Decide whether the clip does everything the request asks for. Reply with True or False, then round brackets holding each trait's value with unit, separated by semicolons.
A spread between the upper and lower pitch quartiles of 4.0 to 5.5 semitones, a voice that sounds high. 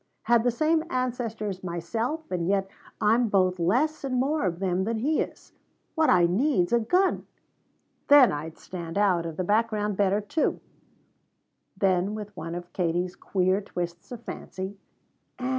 True (5.0 semitones; 205 Hz)